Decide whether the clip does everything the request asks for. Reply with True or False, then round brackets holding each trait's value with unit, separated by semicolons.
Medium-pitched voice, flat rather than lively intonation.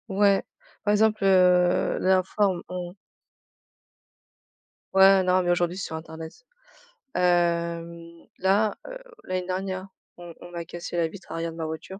True (180 Hz; 2.1 semitones)